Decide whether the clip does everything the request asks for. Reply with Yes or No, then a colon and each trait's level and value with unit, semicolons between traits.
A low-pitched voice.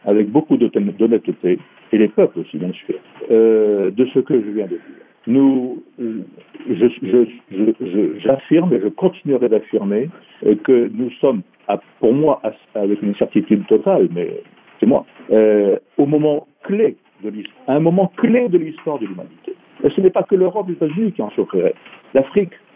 No: medium, 145 Hz